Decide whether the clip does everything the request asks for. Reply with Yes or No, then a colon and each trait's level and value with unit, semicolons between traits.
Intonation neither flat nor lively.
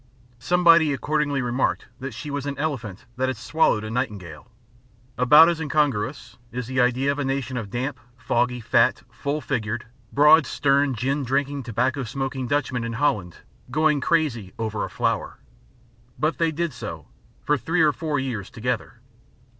Yes: average, 3.5 semitones